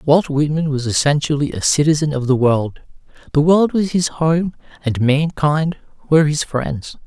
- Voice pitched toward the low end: No, medium, 150 Hz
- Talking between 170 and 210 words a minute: No, average, 160 wpm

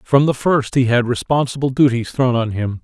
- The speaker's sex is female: No, male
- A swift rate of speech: Yes, fast, 210 wpm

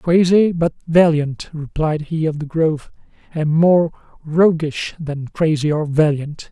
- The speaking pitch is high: No, medium, 160 Hz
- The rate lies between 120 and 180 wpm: Yes, average, 140 wpm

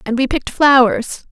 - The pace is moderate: Yes, average, 180 wpm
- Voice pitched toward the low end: No, very high, 255 Hz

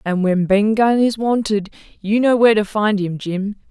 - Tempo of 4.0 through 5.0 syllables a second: Yes, 4.7 syllables/s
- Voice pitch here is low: No, high, 210 Hz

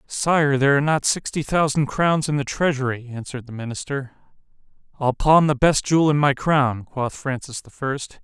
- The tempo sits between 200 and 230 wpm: No, average, 175 wpm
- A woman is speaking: No, male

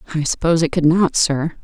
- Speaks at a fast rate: Yes, fast, 220 wpm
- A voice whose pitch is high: No, medium, 165 Hz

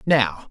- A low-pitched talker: Yes, low, 115 Hz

